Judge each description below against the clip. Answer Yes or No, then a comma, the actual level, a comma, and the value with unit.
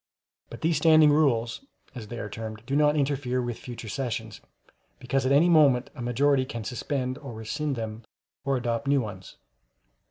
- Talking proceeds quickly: No, average, 170 wpm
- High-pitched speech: No, low, 130 Hz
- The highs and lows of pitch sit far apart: No, average, 3.7 semitones